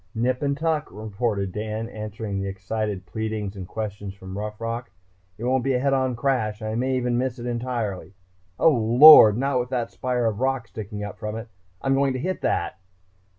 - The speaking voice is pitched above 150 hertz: No, low, 115 Hz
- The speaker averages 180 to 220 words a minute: Yes, average, 195 wpm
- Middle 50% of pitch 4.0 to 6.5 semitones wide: No, average, 3.3 semitones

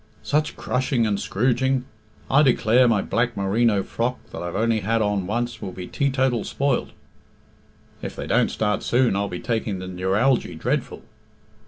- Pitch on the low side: Yes, low, 115 Hz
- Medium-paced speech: Yes, average, 160 wpm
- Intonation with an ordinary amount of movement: Yes, average, 4.1 semitones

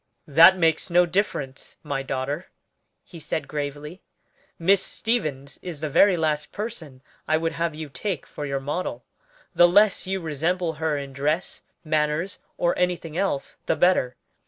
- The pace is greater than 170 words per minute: No, average, 155 wpm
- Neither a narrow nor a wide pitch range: Yes, average, 3.6 semitones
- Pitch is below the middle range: No, medium, 160 Hz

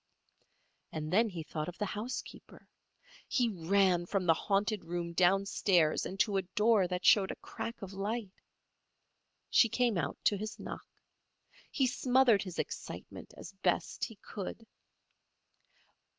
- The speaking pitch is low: No, high, 195 Hz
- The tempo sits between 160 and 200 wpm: No, average, 140 wpm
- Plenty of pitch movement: No, average, 3.7 semitones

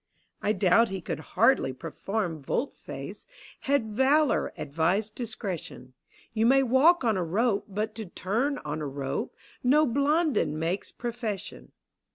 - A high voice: Yes, high, 215 Hz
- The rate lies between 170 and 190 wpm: No, average, 140 wpm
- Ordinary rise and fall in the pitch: No, wide, 6.6 semitones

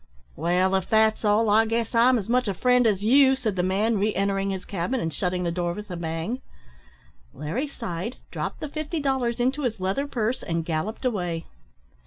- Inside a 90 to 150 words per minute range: No, average, 200 wpm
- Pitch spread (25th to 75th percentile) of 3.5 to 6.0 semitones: Yes, average, 5.3 semitones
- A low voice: No, high, 210 Hz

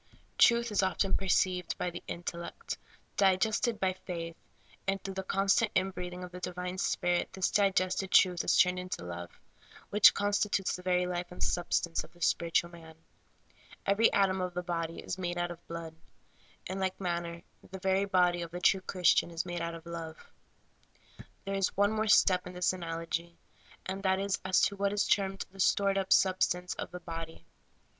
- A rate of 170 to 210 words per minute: Yes, average, 190 wpm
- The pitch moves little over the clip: Yes, narrow, 2.0 semitones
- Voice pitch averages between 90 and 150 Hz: No, medium, 180 Hz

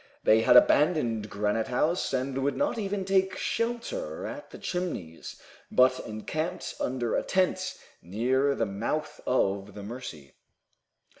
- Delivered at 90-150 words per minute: Yes, slow, 135 wpm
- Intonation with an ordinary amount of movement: No, wide, 8.8 semitones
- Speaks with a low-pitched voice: Yes, low, 130 Hz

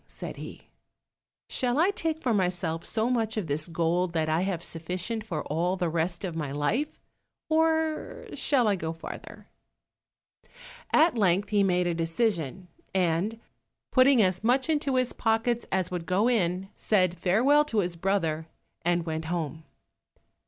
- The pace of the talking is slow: No, average, 155 wpm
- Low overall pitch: No, medium, 185 Hz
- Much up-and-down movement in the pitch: Yes, wide, 5.8 semitones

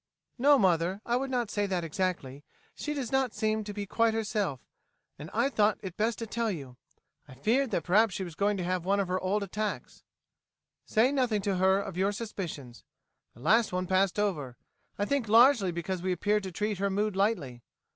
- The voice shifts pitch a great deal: No, average, 3.4 semitones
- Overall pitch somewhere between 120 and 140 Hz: No, high, 200 Hz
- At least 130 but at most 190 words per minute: No, fast, 205 wpm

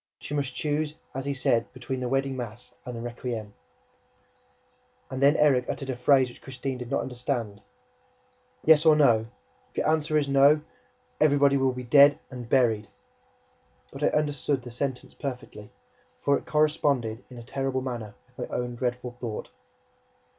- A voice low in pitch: Yes, low, 130 Hz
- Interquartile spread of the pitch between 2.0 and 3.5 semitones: Yes, average, 2.7 semitones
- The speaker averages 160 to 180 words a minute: Yes, average, 170 wpm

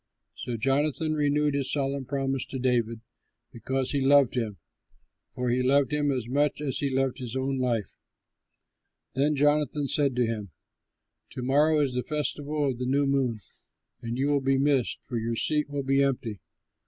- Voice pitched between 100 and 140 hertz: Yes, low, 135 Hz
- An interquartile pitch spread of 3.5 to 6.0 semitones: No, narrow, 2.4 semitones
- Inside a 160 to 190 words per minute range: Yes, average, 175 wpm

